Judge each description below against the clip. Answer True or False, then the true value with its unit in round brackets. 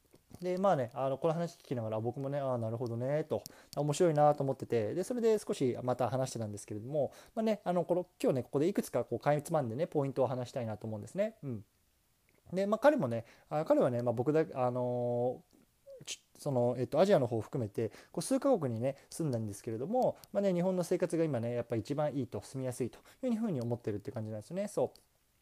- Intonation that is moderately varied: False (6.7 semitones)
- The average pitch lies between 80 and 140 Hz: True (135 Hz)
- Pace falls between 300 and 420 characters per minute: False (445 characters per minute)